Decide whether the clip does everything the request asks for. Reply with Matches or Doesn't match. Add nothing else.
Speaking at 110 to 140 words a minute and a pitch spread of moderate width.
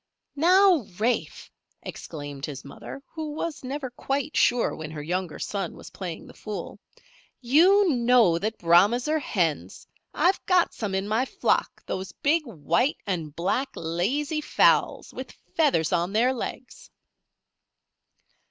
Doesn't match